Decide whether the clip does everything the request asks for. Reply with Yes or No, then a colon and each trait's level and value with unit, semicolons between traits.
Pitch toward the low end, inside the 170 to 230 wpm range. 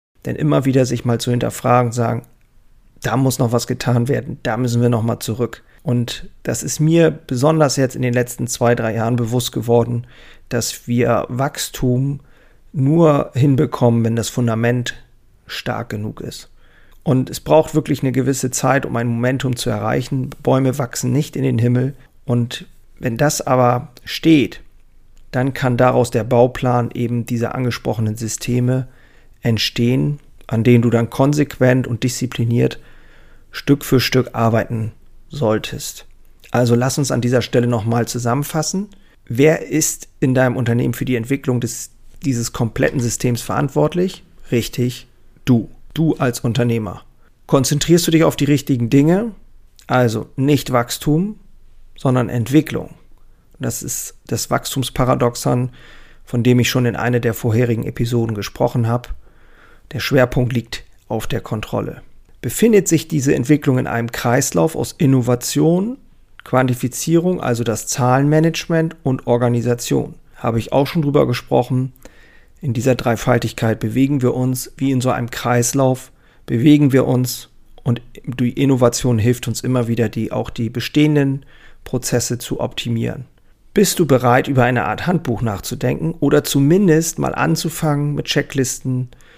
No: low, 125 Hz; average, 140 wpm